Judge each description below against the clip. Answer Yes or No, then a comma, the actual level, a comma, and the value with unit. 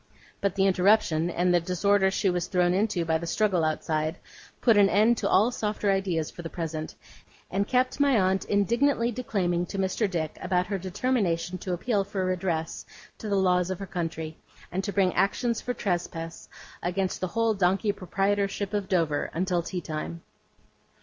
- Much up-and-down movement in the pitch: No, average, 2.7 semitones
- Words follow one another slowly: No, average, 175 wpm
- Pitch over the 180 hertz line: Yes, high, 190 Hz